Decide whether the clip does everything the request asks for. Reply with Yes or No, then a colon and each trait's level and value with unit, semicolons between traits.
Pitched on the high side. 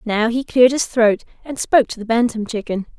Yes: high, 235 Hz